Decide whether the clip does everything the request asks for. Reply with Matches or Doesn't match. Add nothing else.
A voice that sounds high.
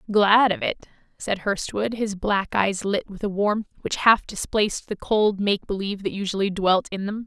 Matches